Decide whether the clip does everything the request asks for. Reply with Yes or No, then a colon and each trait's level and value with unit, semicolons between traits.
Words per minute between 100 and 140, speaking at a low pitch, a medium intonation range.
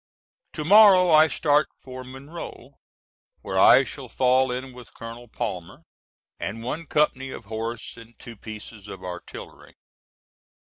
Yes: slow, 135 wpm; low, 125 Hz; average, 4.8 semitones